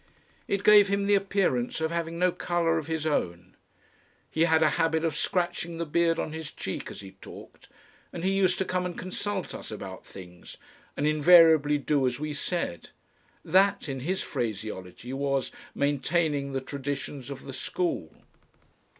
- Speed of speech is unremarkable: Yes, average, 165 wpm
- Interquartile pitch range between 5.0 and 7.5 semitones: No, average, 4.3 semitones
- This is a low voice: No, medium, 160 Hz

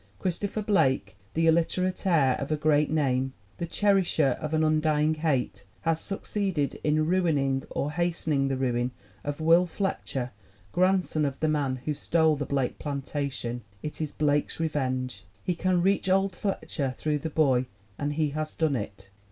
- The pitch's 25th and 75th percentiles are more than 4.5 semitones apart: No, average, 3.6 semitones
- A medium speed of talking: Yes, average, 160 wpm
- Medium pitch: Yes, medium, 155 Hz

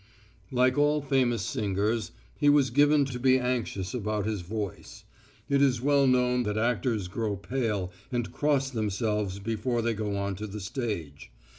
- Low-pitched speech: Yes, low, 115 Hz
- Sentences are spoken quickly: No, average, 160 wpm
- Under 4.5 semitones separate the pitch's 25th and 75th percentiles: Yes, average, 3.9 semitones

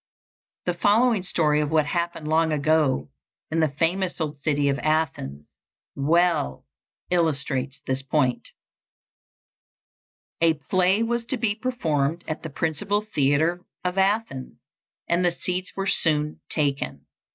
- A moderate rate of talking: No, slow, 130 wpm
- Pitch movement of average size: Yes, average, 3.9 semitones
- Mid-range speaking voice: Yes, medium, 160 Hz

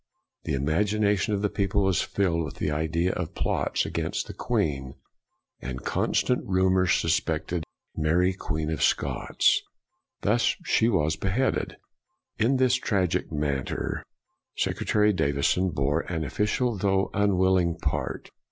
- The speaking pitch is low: Yes, very low, 90 Hz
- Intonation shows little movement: No, average, 4.6 semitones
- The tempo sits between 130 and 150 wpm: Yes, slow, 135 wpm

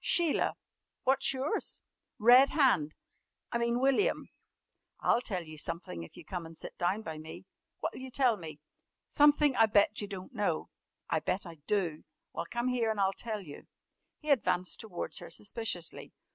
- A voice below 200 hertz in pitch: No, high, 210 Hz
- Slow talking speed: No, average, 170 wpm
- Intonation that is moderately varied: No, wide, 6.6 semitones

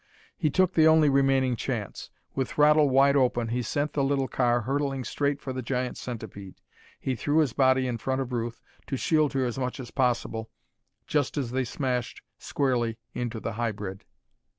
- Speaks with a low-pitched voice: Yes, low, 130 Hz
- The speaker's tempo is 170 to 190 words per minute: Yes, average, 180 wpm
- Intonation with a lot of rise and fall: No, average, 2.7 semitones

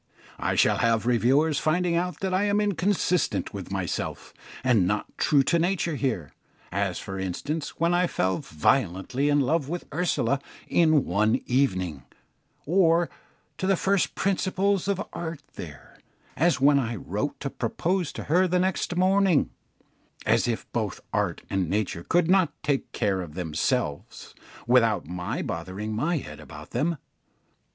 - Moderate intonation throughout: No, wide, 8.7 semitones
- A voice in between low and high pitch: Yes, medium, 145 Hz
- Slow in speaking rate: No, average, 150 wpm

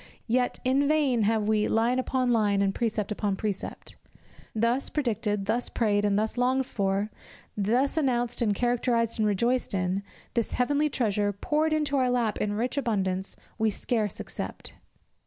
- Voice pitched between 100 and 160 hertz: No, high, 230 Hz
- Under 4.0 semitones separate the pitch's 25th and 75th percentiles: Yes, average, 3.5 semitones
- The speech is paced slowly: No, average, 155 wpm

